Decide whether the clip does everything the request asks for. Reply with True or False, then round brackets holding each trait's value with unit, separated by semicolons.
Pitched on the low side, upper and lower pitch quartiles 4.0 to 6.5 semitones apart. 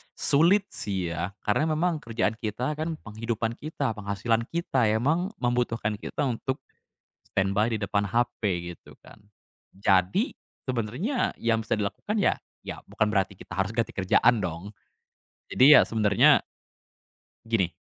True (110 Hz; 4.3 semitones)